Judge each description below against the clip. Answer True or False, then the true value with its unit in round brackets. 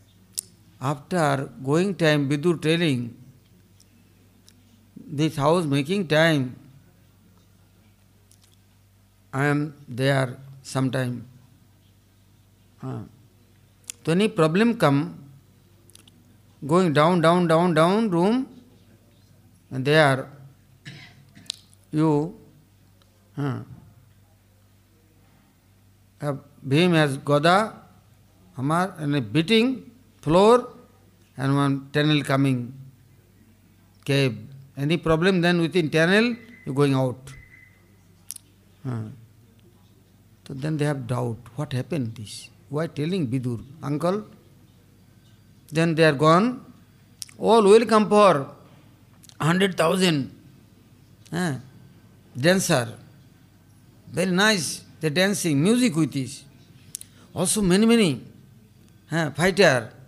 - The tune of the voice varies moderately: False (6.6 semitones)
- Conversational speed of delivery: False (80 wpm)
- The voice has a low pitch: True (130 Hz)